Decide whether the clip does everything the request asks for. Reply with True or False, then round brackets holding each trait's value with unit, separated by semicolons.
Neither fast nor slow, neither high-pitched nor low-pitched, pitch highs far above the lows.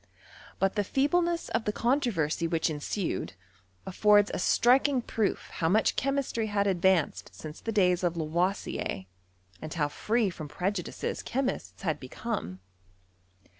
False (150 wpm; 195 Hz; 5.9 semitones)